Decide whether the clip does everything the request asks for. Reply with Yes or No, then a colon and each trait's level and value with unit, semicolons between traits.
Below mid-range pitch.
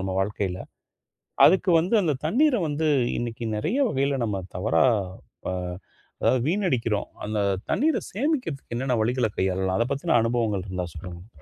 Yes: low, 120 Hz